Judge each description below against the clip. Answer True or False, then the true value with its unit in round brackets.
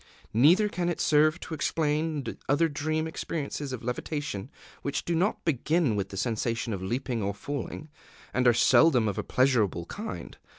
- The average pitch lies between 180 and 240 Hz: False (140 Hz)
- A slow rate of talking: False (165 wpm)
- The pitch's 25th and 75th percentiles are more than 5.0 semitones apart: True (5.5 semitones)